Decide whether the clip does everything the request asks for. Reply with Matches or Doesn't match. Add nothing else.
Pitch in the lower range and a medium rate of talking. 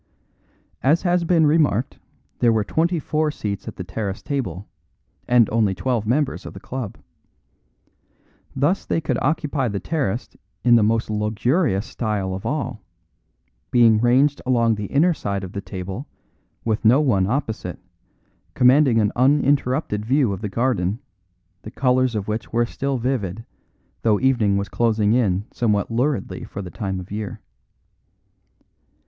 Matches